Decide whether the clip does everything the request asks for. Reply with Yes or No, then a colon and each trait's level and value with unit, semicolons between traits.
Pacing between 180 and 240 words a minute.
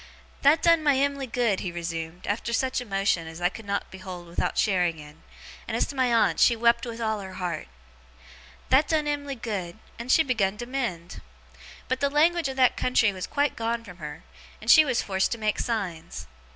Yes: fast, 205 wpm